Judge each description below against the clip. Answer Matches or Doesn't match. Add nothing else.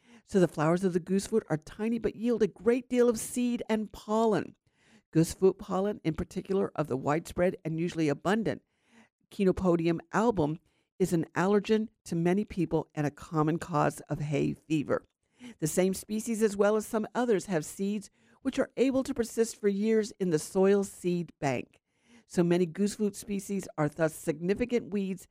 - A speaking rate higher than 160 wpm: Matches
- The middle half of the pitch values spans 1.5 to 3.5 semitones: Doesn't match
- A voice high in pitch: Matches